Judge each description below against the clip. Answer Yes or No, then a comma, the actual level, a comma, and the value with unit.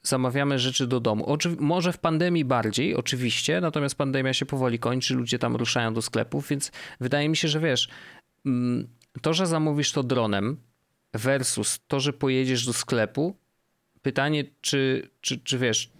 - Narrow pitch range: No, average, 3.4 semitones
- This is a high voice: No, low, 135 Hz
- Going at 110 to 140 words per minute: No, fast, 160 wpm